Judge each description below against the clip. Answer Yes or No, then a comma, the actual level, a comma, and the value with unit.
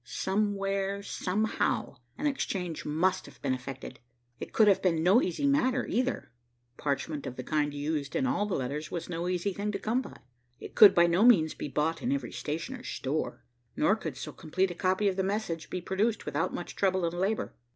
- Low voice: No, medium, 185 Hz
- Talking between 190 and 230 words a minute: Yes, average, 200 wpm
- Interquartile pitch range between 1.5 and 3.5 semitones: No, average, 4.9 semitones